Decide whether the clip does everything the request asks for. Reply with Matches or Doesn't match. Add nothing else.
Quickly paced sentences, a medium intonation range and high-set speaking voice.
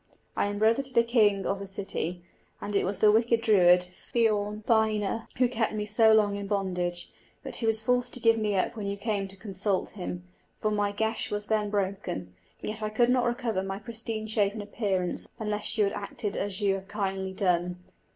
Doesn't match